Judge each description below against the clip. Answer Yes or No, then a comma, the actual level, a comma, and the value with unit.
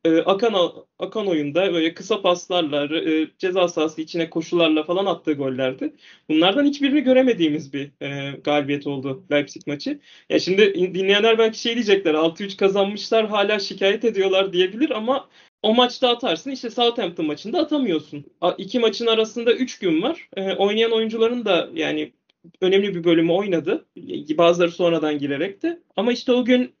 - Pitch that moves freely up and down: Yes, wide, 6.2 semitones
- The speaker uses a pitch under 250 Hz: Yes, high, 190 Hz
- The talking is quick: Yes, fast, 150 wpm